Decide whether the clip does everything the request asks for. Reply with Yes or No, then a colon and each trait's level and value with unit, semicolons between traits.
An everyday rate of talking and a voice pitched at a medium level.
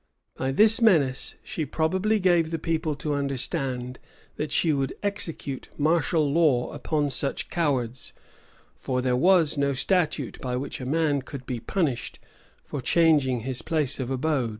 Yes: average, 155 wpm; medium, 145 Hz